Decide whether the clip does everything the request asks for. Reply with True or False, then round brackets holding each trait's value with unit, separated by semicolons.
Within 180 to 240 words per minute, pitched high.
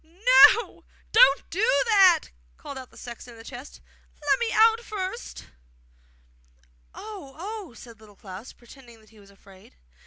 False (155 wpm; 290 Hz)